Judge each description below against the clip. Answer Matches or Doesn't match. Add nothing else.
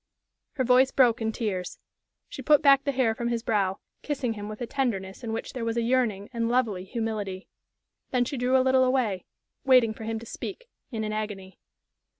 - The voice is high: Matches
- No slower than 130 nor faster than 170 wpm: Doesn't match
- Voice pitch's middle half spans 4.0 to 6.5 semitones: Doesn't match